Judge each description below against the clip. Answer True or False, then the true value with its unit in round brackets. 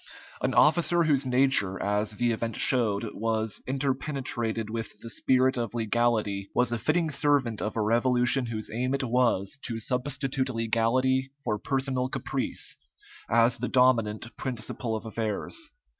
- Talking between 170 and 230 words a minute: False (145 wpm)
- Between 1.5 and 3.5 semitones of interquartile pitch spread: True (2.9 semitones)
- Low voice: True (120 Hz)